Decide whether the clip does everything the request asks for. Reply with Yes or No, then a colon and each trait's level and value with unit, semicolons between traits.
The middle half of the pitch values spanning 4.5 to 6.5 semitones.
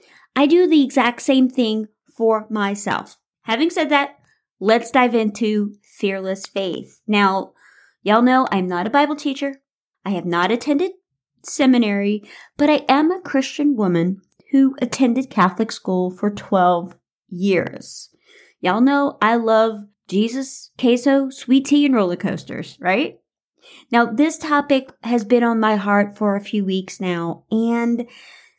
Yes: average, 5.2 semitones